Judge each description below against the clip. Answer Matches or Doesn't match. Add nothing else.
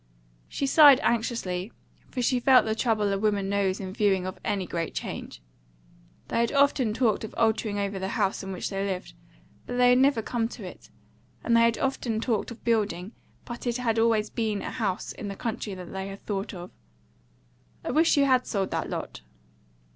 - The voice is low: Doesn't match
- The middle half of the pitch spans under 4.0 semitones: Matches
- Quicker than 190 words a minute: Matches